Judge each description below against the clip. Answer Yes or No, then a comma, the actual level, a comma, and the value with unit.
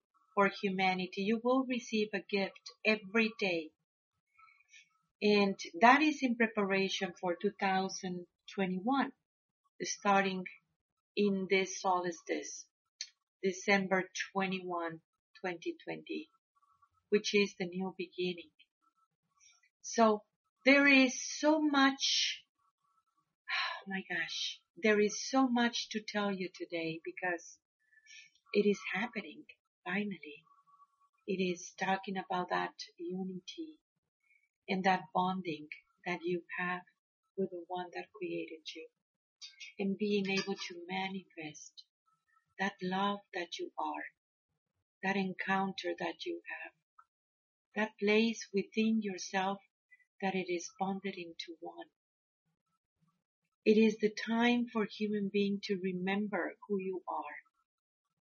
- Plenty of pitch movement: No, average, 4.5 semitones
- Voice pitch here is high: Yes, high, 195 Hz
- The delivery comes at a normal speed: No, slow, 105 wpm